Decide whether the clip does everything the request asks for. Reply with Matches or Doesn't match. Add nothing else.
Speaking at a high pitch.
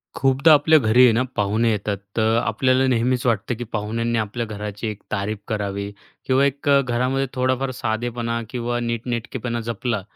Doesn't match